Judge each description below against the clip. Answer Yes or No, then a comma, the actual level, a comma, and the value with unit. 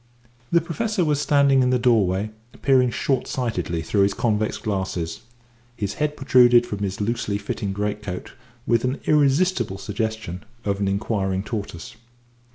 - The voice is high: No, low, 110 Hz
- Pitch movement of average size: Yes, average, 4.6 semitones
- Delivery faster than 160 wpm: No, average, 150 wpm